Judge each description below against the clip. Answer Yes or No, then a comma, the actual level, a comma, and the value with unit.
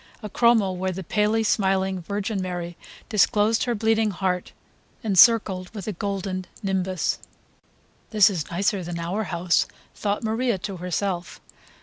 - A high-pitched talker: Yes, high, 195 Hz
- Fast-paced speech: No, slow, 135 wpm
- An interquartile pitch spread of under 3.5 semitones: Yes, average, 2.7 semitones